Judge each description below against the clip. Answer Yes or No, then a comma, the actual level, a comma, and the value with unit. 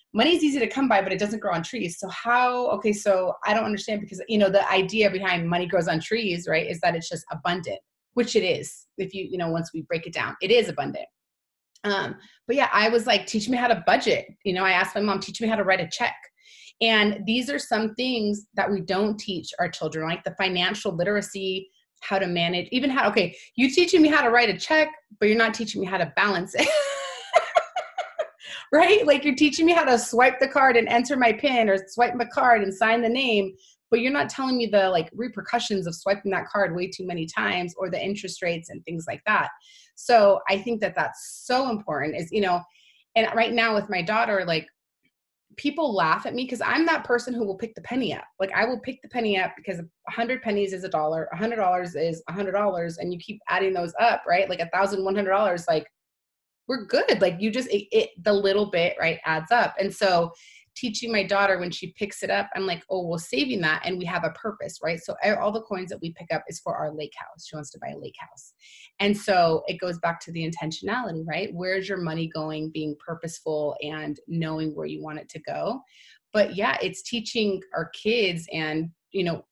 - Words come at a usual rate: No, fast, 235 wpm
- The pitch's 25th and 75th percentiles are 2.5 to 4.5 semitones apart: No, average, 5.1 semitones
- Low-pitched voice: No, high, 200 Hz